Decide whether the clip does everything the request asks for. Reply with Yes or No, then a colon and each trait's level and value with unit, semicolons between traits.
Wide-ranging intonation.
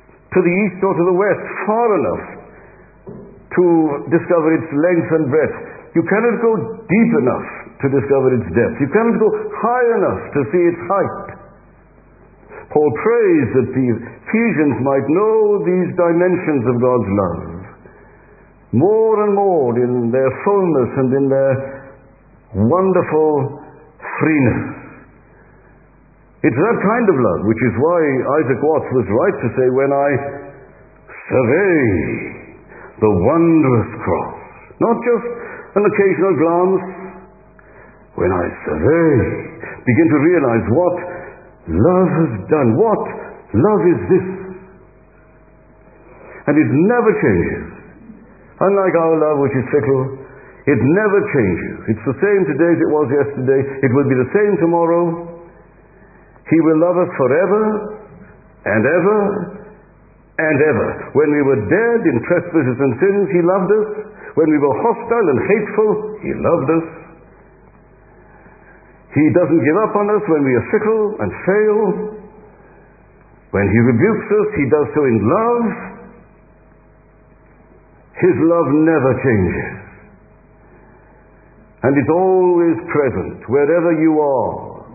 Yes: wide, 6.8 semitones